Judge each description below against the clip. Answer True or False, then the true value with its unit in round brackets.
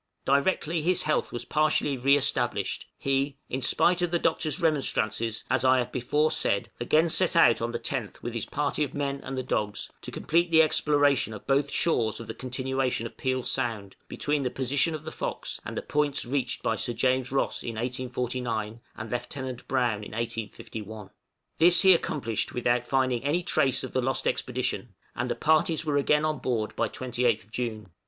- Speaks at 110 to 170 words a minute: False (190 wpm)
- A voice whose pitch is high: False (130 Hz)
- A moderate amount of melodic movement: True (3.8 semitones)